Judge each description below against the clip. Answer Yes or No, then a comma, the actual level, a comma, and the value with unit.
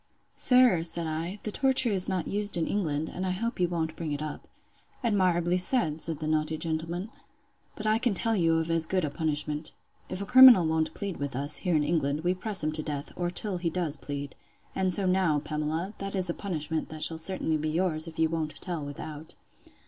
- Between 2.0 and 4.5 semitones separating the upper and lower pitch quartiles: Yes, average, 3.4 semitones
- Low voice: No, medium, 165 Hz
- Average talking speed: No, fast, 210 wpm